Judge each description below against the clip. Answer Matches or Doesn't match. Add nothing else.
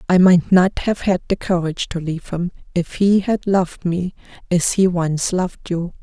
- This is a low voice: Doesn't match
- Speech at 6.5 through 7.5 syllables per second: Doesn't match